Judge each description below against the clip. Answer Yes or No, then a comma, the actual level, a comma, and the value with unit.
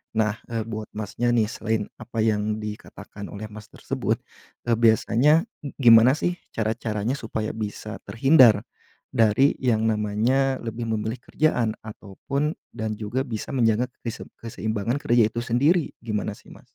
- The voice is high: No, low, 115 Hz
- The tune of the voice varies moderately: No, narrow, 2.3 semitones